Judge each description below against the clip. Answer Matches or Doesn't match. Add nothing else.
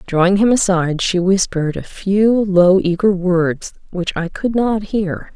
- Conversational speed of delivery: Matches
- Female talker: Matches